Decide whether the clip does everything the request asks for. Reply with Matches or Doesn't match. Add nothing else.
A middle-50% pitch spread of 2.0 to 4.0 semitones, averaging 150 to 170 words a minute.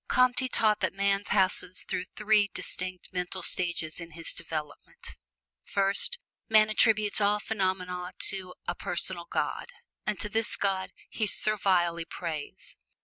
Doesn't match